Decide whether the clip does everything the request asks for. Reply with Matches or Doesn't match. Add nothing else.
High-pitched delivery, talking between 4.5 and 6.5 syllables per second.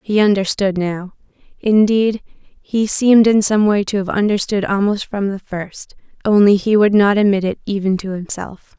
Matches